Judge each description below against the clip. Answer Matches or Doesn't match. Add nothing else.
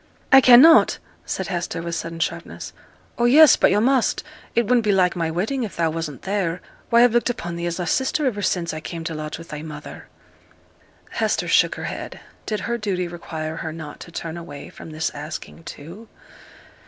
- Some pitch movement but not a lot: Doesn't match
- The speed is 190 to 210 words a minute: Matches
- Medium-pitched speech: Matches